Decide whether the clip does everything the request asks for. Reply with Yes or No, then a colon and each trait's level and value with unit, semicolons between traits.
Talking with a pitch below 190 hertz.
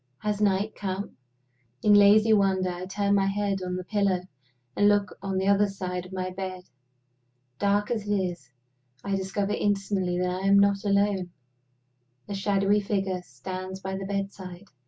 No: high, 195 Hz